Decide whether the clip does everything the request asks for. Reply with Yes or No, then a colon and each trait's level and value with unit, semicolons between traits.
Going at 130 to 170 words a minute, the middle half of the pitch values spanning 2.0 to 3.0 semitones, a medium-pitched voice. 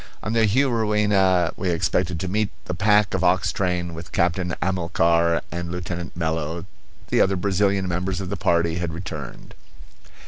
No: average, 150 wpm; narrow, 2.5 semitones; very low, 90 Hz